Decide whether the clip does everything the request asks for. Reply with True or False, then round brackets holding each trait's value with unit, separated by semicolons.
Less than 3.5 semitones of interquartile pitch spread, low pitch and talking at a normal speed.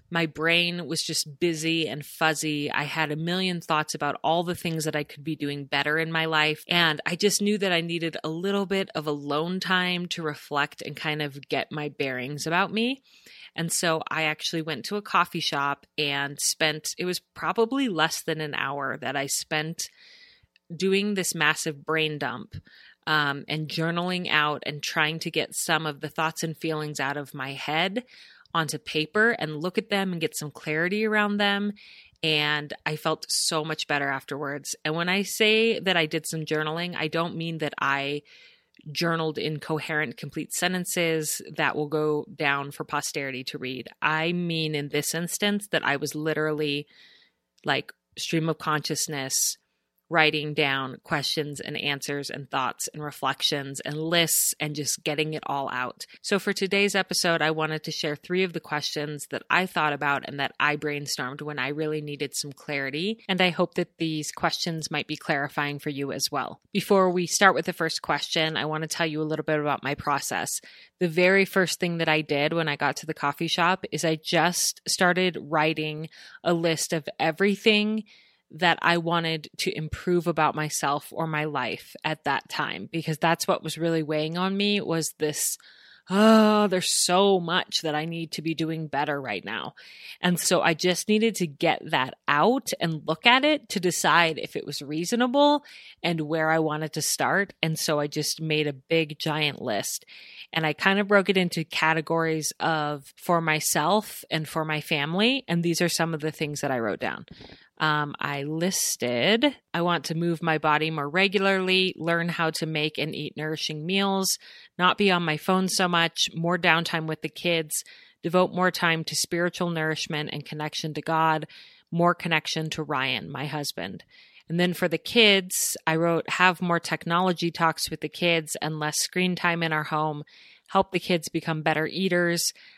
False (2.8 semitones; 160 Hz; 190 wpm)